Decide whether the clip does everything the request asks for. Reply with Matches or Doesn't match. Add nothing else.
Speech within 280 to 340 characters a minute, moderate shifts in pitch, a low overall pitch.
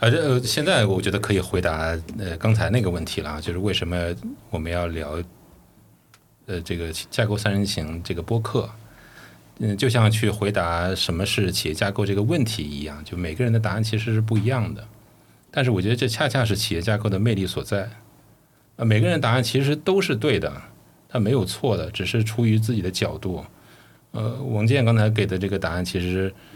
Matches